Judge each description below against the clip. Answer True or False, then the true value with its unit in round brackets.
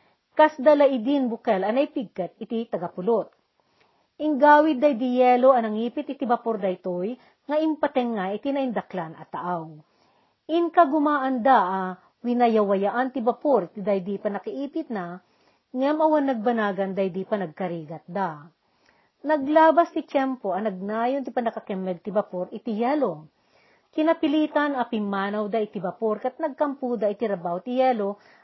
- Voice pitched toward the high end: True (235 Hz)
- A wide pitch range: True (6.0 semitones)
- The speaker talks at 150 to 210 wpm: False (135 wpm)